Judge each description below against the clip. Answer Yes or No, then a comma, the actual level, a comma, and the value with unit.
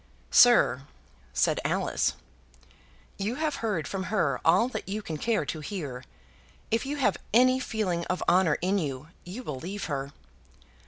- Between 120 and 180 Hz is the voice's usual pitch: No, high, 190 Hz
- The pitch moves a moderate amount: No, wide, 6.7 semitones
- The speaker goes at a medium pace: Yes, average, 155 wpm